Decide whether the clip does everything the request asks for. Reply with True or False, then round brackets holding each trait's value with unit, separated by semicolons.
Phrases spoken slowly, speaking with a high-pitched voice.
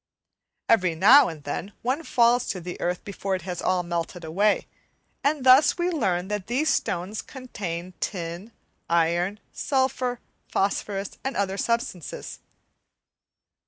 True (130 wpm; 200 Hz)